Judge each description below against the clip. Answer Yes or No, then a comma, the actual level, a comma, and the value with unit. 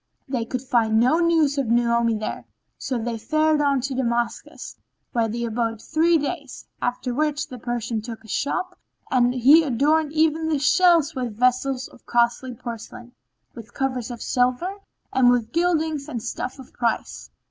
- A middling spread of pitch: Yes, average, 4.1 semitones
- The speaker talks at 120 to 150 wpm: No, average, 165 wpm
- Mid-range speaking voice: No, very high, 255 Hz